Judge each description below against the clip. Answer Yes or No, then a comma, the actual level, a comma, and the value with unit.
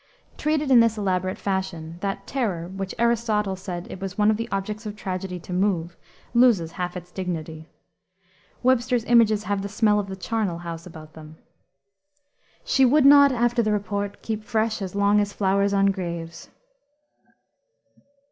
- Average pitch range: Yes, average, 3.6 semitones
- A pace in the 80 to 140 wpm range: No, average, 160 wpm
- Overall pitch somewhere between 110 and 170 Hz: No, high, 200 Hz